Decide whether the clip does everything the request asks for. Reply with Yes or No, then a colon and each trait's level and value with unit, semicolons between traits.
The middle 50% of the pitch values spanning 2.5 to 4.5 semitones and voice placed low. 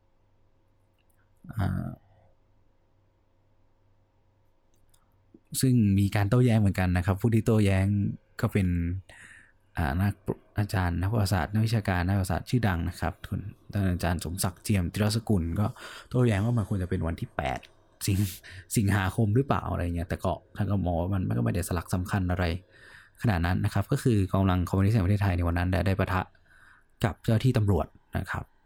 Yes: average, 2.8 semitones; low, 100 Hz